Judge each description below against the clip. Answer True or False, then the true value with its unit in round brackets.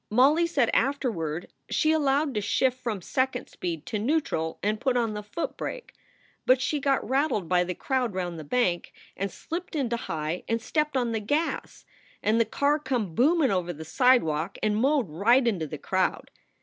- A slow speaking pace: False (185 wpm)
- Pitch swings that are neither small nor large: False (6.7 semitones)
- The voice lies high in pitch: True (235 Hz)